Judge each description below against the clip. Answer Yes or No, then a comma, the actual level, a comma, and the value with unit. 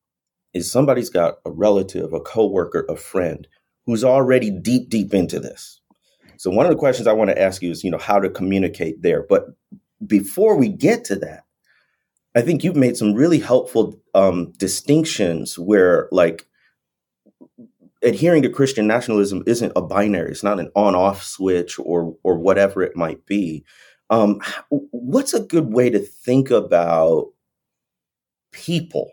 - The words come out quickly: No, average, 155 wpm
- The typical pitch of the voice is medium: No, low, 120 Hz